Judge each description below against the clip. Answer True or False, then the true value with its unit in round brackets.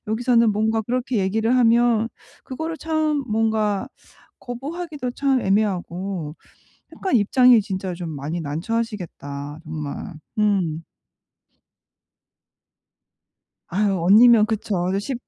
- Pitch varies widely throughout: False (5.0 semitones)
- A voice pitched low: False (215 Hz)